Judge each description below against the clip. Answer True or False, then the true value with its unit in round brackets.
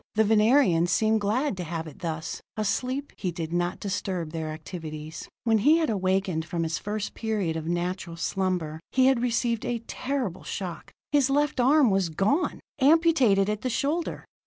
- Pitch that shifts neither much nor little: False (6.6 semitones)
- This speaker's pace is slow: False (170 wpm)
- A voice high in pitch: True (200 Hz)